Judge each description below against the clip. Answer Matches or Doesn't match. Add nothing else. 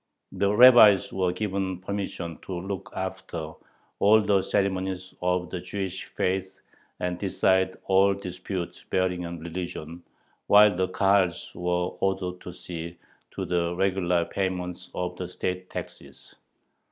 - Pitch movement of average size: Doesn't match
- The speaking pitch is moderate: Doesn't match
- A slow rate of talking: Matches